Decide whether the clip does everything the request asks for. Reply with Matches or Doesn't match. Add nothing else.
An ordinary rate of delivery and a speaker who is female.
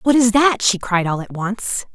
Doesn't match